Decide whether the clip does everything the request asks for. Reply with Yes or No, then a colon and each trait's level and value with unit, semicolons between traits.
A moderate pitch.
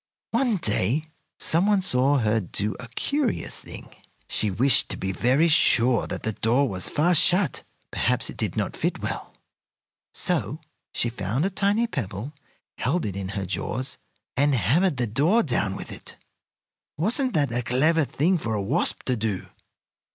No: low, 130 Hz